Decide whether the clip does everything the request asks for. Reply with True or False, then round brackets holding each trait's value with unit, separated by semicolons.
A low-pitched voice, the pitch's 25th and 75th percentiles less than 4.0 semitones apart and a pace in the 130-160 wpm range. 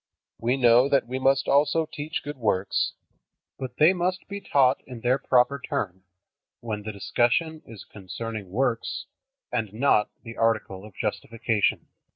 False (120 Hz; 4.3 semitones; 150 wpm)